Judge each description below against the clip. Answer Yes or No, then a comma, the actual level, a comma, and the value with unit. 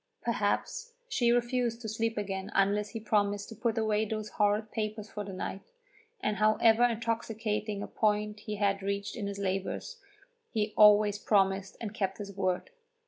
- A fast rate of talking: No, average, 165 wpm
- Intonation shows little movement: Yes, narrow, 1.9 semitones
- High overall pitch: Yes, high, 210 Hz